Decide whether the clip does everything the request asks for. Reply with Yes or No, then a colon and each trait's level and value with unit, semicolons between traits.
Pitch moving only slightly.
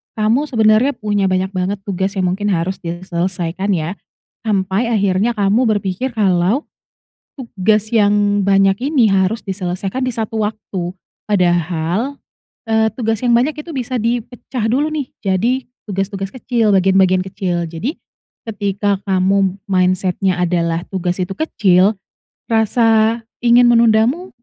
No: average, 3.5 semitones